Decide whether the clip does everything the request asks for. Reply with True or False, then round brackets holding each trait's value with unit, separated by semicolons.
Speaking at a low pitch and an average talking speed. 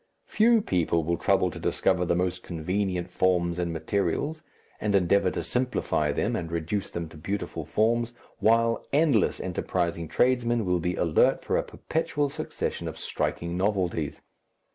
True (95 Hz; 150 wpm)